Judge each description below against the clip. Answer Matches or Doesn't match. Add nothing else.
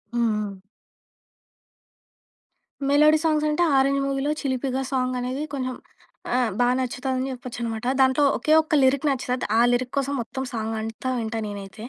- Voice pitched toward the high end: Matches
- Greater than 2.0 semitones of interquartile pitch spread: Matches